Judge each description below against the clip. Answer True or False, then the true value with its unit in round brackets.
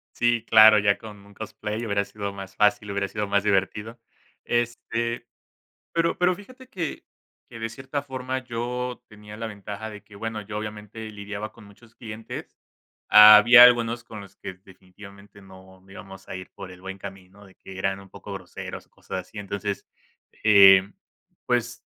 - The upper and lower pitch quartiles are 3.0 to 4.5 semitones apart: False (2.5 semitones)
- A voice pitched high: False (105 Hz)